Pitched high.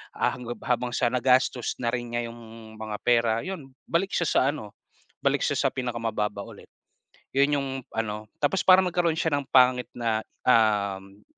No: low, 120 Hz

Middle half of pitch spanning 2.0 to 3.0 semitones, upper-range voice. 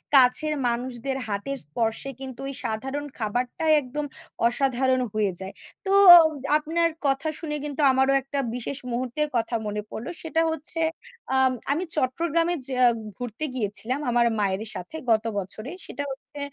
No: average, 4.1 semitones; very high, 260 Hz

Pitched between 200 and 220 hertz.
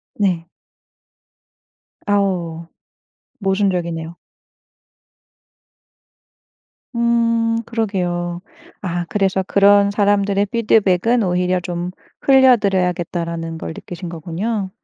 No: high, 190 Hz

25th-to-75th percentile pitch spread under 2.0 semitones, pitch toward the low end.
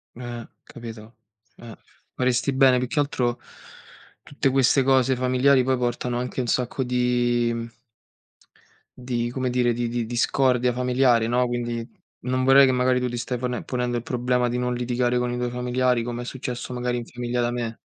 Yes: narrow, 0.9 semitones; low, 125 Hz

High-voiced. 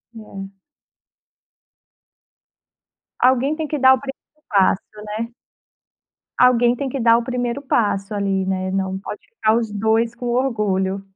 Yes: high, 230 Hz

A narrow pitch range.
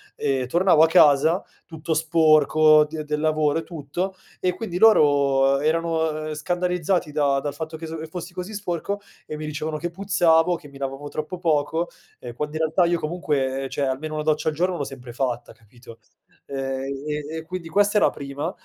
No: average, 3.1 semitones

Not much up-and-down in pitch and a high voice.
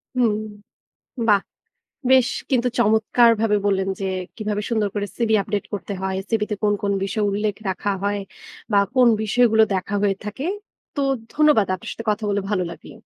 Yes: narrow, 2.1 semitones; high, 210 Hz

